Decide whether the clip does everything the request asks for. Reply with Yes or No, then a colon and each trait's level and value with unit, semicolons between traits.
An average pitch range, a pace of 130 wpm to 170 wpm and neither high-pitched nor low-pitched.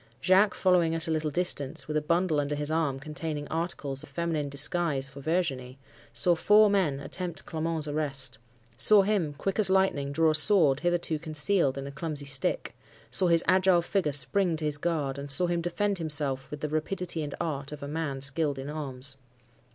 No: average, 3.6 semitones; average, 180 wpm; medium, 155 Hz